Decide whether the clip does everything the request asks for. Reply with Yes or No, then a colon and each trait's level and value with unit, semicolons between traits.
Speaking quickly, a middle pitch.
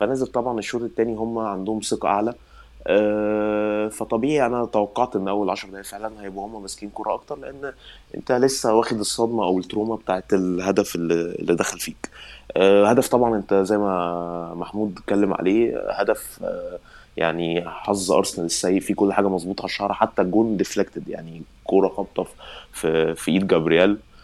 No: fast, 150 wpm; low, 105 Hz